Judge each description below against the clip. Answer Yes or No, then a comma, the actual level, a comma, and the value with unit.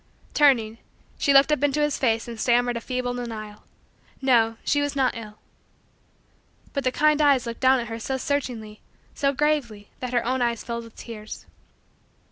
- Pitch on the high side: Yes, high, 245 Hz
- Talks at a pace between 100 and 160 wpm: No, average, 175 wpm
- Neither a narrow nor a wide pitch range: Yes, average, 3.3 semitones